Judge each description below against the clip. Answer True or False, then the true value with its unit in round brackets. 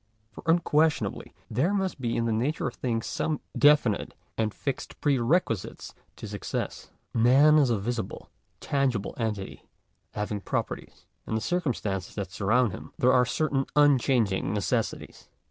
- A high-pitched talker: False (125 Hz)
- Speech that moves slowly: False (145 wpm)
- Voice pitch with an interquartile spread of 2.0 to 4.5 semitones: False (5.1 semitones)